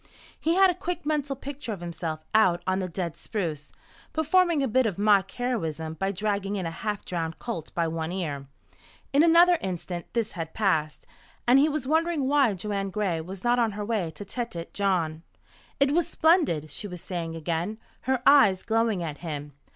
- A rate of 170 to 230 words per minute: Yes, average, 190 wpm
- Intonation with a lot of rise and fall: Yes, wide, 7.5 semitones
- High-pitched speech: Yes, high, 200 Hz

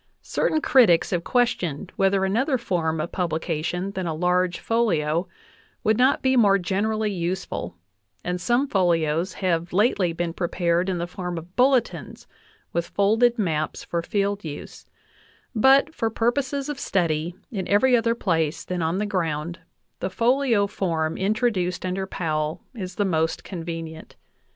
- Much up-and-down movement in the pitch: No, average, 4.5 semitones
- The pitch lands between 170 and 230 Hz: Yes, medium, 185 Hz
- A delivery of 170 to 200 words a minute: No, average, 145 wpm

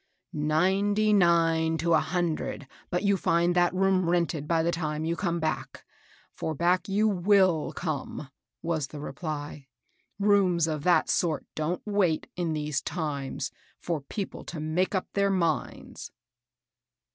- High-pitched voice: No, medium, 170 Hz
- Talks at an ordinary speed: Yes, average, 155 wpm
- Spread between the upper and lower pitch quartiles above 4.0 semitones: No, average, 3.0 semitones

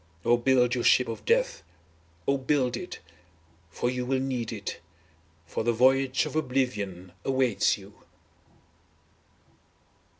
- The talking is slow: Yes, slow, 125 wpm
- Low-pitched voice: Yes, low, 125 Hz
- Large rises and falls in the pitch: No, narrow, 2.6 semitones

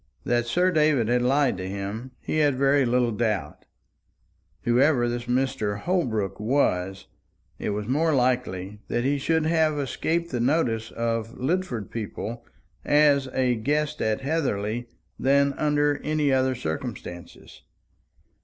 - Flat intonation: No, average, 4.5 semitones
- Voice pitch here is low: Yes, low, 125 Hz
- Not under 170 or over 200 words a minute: No, slow, 135 wpm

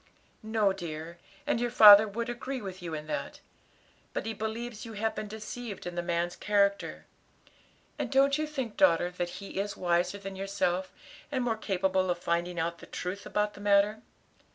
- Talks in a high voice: Yes, high, 200 Hz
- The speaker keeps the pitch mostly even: No, average, 3.9 semitones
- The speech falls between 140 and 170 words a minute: No, average, 180 wpm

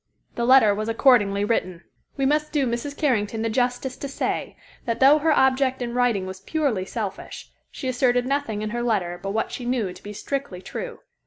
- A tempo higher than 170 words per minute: Yes, average, 195 wpm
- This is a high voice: Yes, high, 240 Hz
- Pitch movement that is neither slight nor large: Yes, average, 4.4 semitones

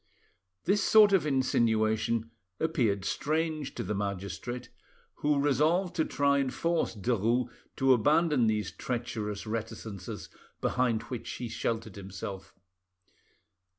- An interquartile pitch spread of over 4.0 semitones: Yes, average, 5.2 semitones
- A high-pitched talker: No, low, 120 Hz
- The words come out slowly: Yes, slow, 115 wpm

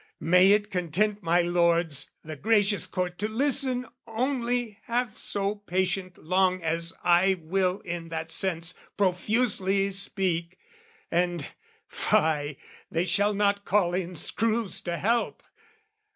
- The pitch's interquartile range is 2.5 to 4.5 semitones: Yes, average, 3.4 semitones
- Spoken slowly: Yes, slow, 125 wpm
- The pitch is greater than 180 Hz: Yes, high, 190 Hz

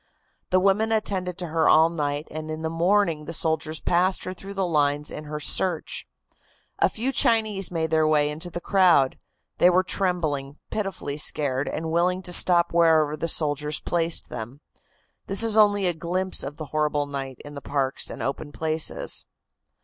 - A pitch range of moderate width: Yes, average, 3.6 semitones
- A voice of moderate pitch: Yes, medium, 160 Hz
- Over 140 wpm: Yes, average, 180 wpm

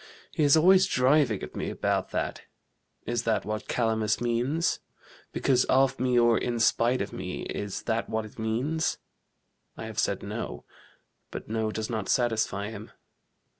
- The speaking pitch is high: No, low, 115 Hz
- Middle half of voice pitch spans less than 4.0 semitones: Yes, average, 2.8 semitones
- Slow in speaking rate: No, average, 160 wpm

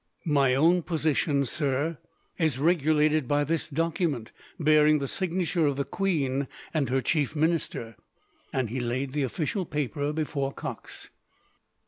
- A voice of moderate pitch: Yes, medium, 150 Hz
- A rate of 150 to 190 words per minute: No, slow, 135 wpm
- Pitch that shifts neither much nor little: Yes, average, 3.0 semitones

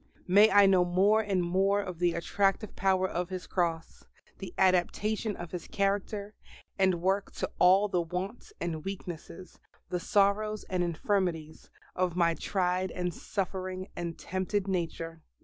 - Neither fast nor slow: Yes, average, 150 wpm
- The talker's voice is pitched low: No, medium, 185 Hz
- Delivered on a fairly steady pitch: Yes, narrow, 2.1 semitones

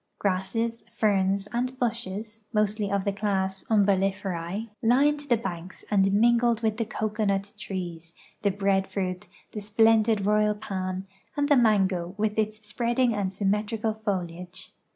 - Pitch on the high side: Yes, high, 205 Hz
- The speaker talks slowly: Yes, slow, 130 wpm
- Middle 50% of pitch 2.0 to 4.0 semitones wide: Yes, narrow, 2.6 semitones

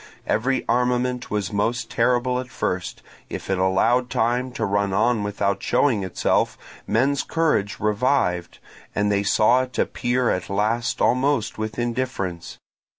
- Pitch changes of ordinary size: Yes, average, 3.9 semitones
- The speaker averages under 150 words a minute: Yes, average, 140 wpm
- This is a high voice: No, low, 115 Hz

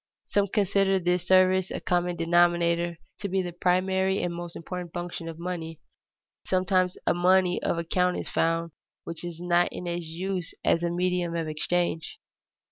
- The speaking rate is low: No, average, 165 wpm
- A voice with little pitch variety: Yes, narrow, 1.4 semitones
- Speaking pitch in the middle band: Yes, medium, 175 Hz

